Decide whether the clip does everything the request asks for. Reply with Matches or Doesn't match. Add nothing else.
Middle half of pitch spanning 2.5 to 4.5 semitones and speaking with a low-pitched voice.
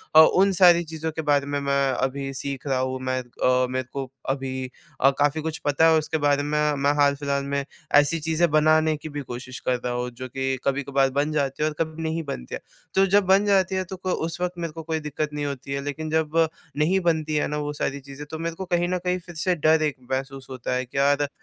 Doesn't match